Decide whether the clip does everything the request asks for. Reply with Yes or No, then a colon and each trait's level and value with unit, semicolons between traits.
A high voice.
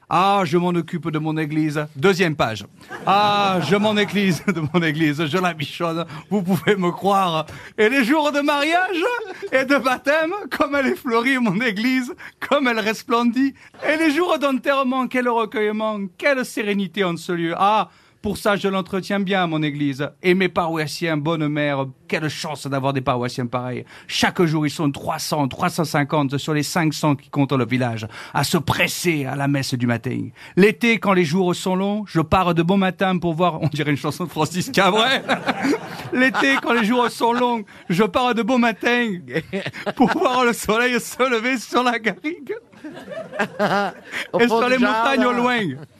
Yes: high, 195 Hz